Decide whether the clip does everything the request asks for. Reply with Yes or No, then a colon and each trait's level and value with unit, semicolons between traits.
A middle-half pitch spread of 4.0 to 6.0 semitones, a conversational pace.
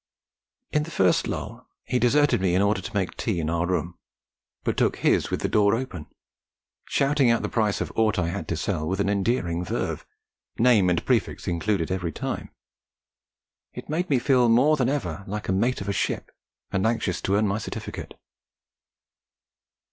Yes: average, 5.2 semitones; average, 185 wpm